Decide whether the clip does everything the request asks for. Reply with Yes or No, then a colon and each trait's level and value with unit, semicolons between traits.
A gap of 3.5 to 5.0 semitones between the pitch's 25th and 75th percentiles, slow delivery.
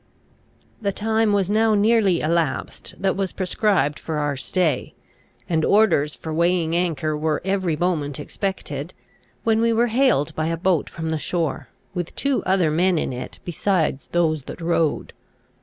No: average, 4.1 semitones; average, 155 wpm